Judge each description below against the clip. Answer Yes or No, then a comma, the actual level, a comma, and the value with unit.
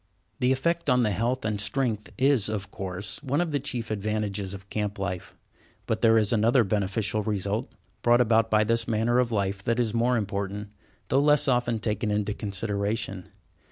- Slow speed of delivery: No, average, 180 wpm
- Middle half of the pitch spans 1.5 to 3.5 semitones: Yes, average, 3.1 semitones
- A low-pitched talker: Yes, low, 110 Hz